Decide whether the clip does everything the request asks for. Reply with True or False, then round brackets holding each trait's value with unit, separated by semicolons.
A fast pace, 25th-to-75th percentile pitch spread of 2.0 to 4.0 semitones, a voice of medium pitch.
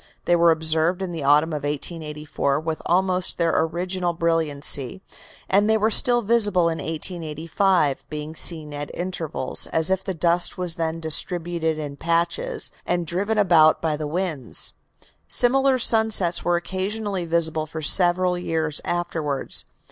False (150 wpm; 2.8 semitones; 170 Hz)